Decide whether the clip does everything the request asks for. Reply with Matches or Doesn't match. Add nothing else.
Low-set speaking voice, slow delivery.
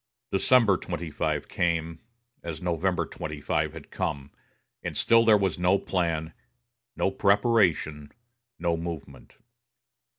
Matches